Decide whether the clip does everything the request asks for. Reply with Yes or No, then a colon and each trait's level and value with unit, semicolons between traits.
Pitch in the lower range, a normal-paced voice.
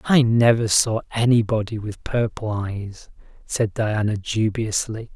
No: low, 110 Hz; slow, 115 wpm